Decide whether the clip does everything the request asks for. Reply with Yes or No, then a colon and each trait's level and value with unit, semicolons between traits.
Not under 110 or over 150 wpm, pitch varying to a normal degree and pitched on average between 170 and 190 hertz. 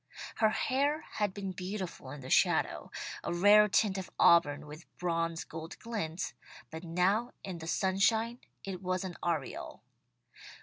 Yes: average, 145 wpm; average, 3.9 semitones; medium, 185 Hz